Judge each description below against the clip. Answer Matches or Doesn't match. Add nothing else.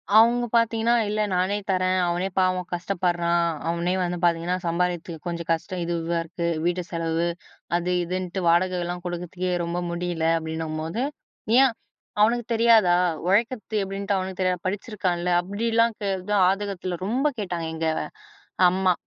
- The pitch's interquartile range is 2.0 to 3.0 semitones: Matches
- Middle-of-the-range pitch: Matches